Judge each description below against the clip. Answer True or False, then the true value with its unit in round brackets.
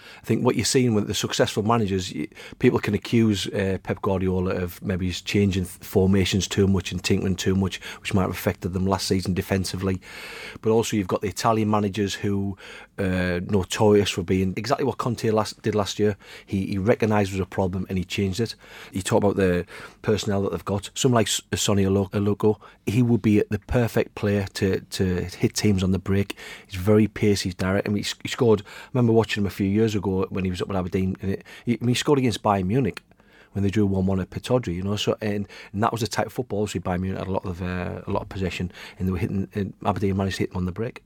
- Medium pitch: False (100 Hz)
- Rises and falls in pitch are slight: True (2.1 semitones)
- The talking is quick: True (240 wpm)